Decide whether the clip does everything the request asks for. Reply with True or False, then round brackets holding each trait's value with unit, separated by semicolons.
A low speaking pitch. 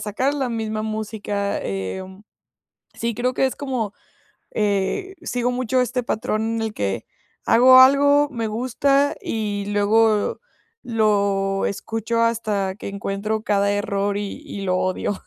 False (220 Hz)